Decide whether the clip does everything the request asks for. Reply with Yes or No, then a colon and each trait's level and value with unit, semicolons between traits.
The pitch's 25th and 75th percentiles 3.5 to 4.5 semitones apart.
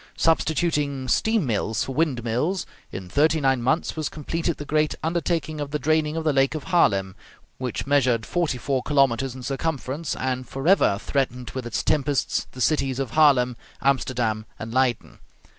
Yes: average, 3.8 semitones